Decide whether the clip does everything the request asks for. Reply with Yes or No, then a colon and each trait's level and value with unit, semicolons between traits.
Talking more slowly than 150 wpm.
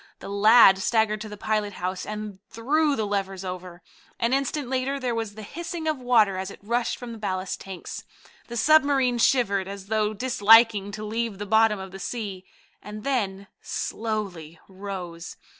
No: average, 175 wpm